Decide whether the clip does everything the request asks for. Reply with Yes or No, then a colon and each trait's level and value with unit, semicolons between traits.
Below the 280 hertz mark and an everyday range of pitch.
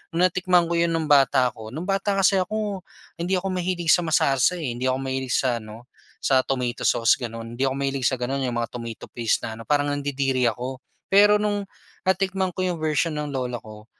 No: medium, 140 Hz; wide, 6.5 semitones